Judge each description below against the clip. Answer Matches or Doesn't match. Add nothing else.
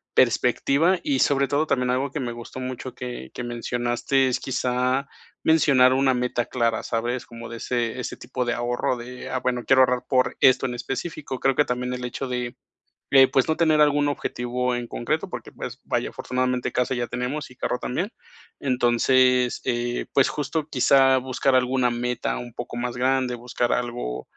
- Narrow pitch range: Matches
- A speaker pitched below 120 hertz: Doesn't match